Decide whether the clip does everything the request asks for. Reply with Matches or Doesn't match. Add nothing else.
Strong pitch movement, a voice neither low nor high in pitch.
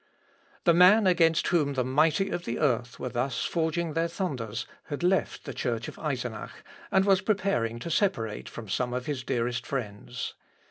Matches